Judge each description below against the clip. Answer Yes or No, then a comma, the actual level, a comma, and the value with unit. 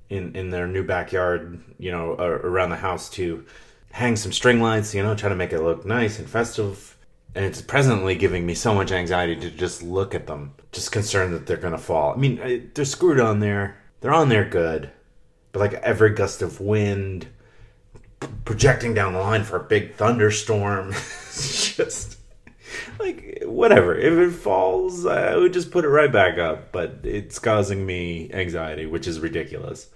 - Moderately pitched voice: No, low, 100 Hz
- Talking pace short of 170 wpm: No, average, 185 wpm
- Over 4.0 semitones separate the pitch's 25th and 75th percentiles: Yes, average, 4.4 semitones